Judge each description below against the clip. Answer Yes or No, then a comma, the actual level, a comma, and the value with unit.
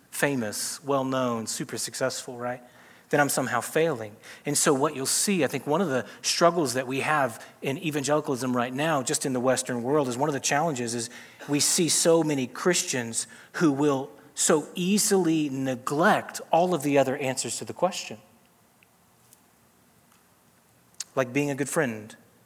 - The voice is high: No, medium, 140 Hz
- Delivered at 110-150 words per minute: No, average, 165 wpm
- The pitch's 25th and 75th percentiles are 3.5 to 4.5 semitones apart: Yes, average, 3.9 semitones